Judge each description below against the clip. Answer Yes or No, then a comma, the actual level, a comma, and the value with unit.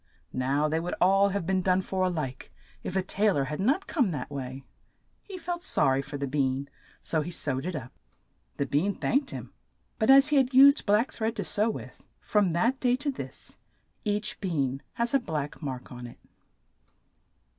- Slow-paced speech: No, average, 200 wpm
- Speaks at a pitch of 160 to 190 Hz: Yes, medium, 185 Hz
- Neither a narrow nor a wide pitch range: No, wide, 8.6 semitones